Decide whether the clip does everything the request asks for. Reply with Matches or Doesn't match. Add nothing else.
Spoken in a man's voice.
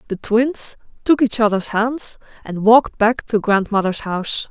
Doesn't match